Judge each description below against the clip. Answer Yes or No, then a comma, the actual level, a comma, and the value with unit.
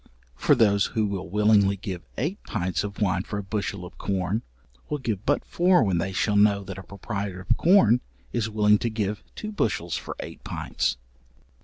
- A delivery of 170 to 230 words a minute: Yes, average, 190 wpm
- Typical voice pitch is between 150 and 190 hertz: No, low, 105 Hz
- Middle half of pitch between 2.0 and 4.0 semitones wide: Yes, narrow, 2.5 semitones